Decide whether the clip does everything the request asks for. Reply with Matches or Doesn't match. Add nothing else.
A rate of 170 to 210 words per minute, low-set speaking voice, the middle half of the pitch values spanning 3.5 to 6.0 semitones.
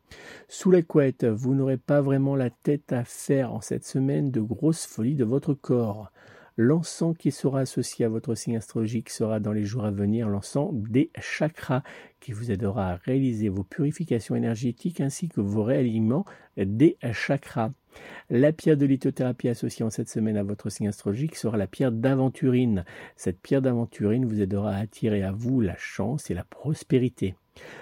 Matches